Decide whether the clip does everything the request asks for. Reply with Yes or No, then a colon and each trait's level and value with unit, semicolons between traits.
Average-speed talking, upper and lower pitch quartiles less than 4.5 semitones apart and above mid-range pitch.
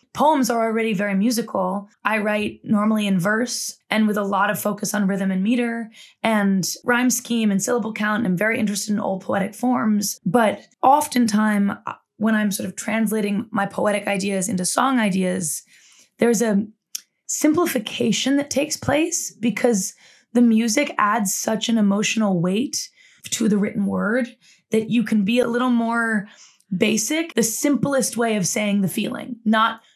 Yes: average, 160 wpm; average, 2.8 semitones; high, 220 Hz